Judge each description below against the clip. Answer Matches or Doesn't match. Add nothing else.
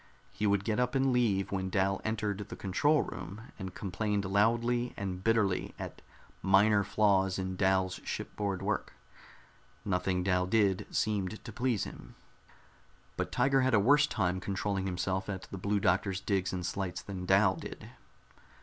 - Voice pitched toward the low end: Matches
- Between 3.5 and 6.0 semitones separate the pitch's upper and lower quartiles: Doesn't match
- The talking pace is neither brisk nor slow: Matches